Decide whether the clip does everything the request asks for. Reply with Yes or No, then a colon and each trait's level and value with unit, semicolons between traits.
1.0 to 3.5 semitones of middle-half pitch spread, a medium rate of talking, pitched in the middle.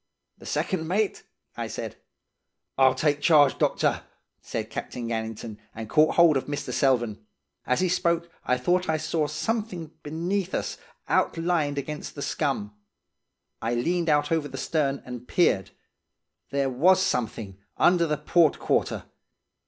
No: average, 5.1 semitones; average, 145 wpm; medium, 150 Hz